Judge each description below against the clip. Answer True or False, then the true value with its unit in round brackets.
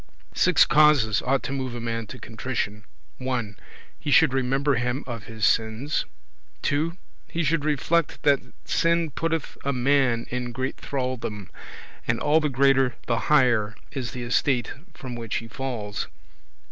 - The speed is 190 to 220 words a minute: False (155 wpm)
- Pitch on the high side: False (130 Hz)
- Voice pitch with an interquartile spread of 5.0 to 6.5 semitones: False (3.5 semitones)